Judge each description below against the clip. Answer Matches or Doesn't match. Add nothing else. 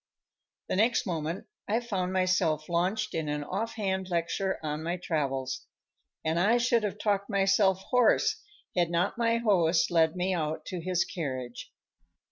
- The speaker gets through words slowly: Doesn't match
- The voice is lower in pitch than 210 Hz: Matches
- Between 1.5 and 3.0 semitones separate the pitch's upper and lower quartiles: Doesn't match